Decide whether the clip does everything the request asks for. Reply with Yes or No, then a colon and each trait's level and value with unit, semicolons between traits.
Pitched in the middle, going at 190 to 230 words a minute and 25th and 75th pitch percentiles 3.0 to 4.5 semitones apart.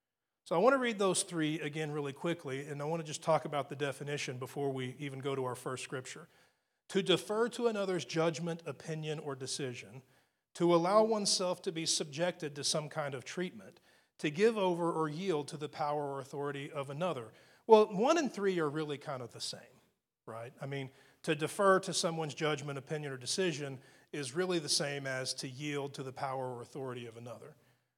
Yes: medium, 150 Hz; average, 200 wpm; average, 4.1 semitones